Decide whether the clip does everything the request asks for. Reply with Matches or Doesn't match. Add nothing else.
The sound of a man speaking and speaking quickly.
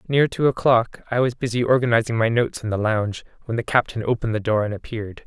Matches